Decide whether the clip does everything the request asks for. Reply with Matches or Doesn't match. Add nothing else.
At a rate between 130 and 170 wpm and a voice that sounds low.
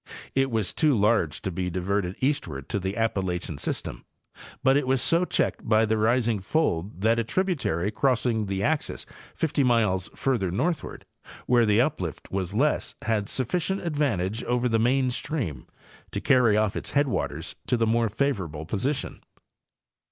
Matches